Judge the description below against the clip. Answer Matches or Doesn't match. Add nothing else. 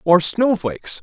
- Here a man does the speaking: Matches